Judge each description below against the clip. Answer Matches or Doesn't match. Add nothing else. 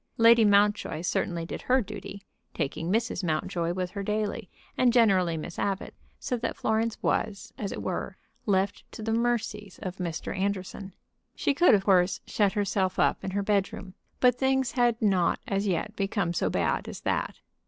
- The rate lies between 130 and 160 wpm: Doesn't match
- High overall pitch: Matches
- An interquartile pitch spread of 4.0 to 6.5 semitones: Doesn't match